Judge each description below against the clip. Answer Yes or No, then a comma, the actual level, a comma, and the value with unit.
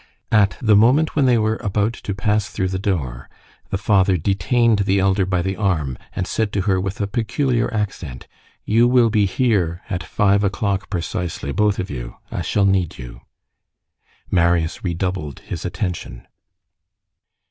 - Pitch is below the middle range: Yes, low, 100 Hz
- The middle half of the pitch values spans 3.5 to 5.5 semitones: No, average, 3.0 semitones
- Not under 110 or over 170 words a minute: Yes, average, 160 wpm